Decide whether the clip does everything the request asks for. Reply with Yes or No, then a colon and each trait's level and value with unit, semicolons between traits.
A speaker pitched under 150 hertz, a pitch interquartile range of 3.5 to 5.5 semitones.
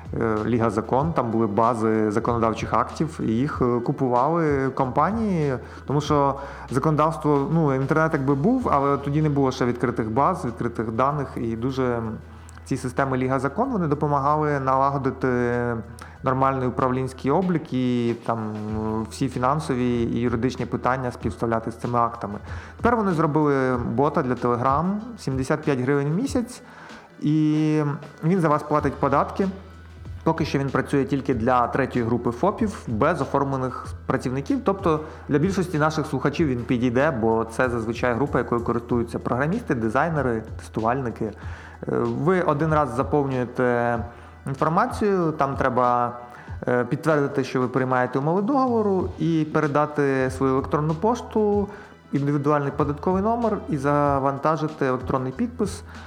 Yes: low, 135 Hz; average, 4.0 semitones